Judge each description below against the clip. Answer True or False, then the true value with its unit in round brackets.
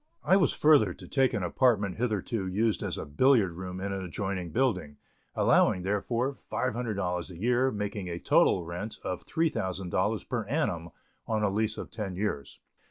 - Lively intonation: False (4.7 semitones)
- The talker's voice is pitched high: False (100 Hz)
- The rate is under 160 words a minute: False (165 wpm)